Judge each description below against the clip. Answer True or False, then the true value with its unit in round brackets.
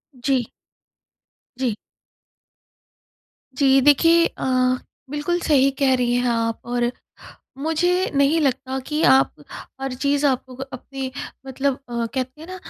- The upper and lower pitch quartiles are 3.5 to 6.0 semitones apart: False (2.6 semitones)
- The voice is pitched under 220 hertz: False (270 Hz)